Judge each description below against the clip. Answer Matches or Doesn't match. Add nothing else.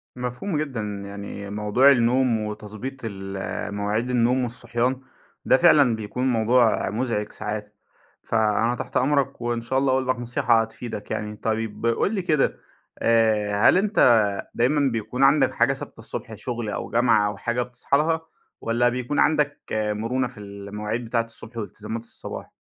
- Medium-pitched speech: Doesn't match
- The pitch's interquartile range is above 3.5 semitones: Doesn't match